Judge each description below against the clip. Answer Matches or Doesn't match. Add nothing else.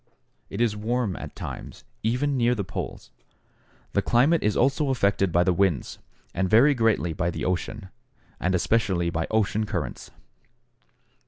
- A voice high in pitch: Doesn't match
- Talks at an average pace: Matches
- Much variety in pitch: Doesn't match